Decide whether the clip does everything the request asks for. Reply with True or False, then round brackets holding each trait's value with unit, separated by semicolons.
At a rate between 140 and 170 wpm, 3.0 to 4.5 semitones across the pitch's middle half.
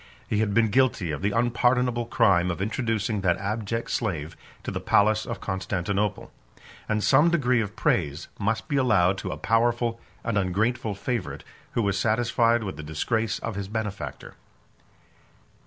True (155 wpm; 3.3 semitones)